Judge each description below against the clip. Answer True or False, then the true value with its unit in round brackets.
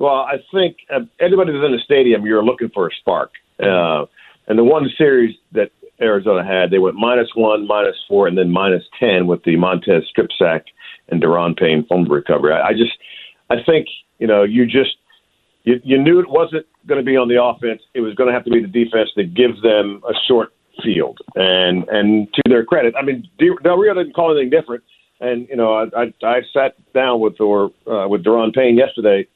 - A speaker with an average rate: False (215 wpm)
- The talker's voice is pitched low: True (120 Hz)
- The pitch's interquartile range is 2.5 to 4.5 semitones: False (5.0 semitones)